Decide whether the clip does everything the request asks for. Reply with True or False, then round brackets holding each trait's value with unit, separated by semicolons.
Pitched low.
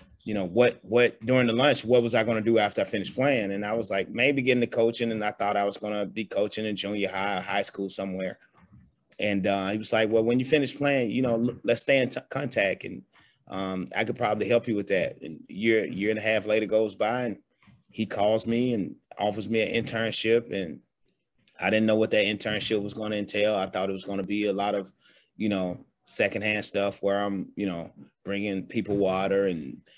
True (105 Hz)